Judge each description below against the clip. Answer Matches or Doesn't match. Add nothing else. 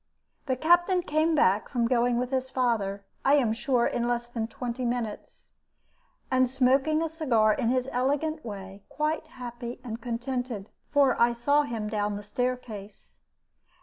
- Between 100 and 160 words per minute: Matches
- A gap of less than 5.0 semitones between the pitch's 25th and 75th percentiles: Matches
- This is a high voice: Matches